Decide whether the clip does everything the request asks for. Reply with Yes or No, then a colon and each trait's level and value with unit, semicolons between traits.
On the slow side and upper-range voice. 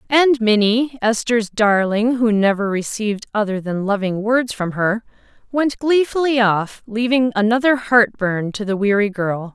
Yes: slow, 130 wpm; high, 220 Hz